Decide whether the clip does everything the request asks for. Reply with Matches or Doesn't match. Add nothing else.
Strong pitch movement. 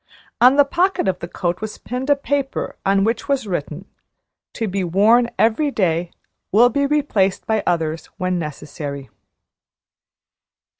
Matches